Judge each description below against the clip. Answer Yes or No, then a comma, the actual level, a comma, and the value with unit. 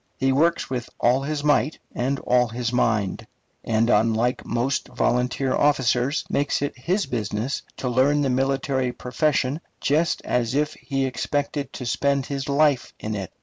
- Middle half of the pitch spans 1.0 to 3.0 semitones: Yes, average, 2.7 semitones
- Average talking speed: Yes, average, 155 wpm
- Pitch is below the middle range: Yes, low, 130 Hz